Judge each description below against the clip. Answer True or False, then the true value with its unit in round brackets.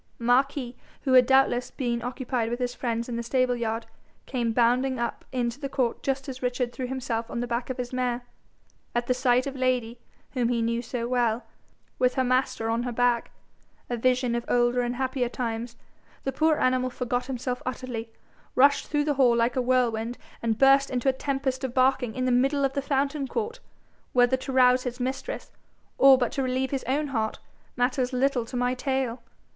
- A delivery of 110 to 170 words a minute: False (195 wpm)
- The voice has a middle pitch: False (250 Hz)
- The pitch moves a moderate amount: False (1.7 semitones)